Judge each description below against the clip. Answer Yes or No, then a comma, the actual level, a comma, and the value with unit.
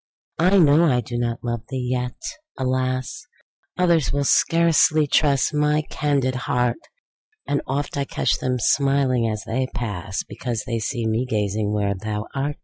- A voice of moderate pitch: No, low, 130 Hz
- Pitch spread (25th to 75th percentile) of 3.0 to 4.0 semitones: Yes, average, 3.5 semitones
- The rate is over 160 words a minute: No, average, 145 wpm